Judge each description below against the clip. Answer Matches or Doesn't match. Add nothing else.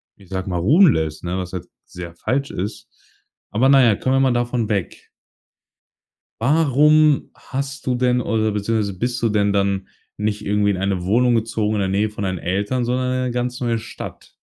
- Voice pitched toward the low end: Matches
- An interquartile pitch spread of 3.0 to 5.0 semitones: Matches